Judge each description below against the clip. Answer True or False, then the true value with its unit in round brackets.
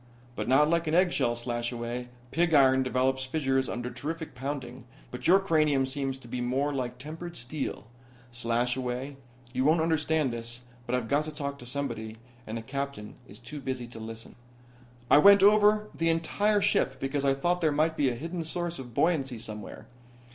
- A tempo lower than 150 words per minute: False (180 wpm)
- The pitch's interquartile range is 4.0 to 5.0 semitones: True (4.4 semitones)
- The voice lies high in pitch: False (135 Hz)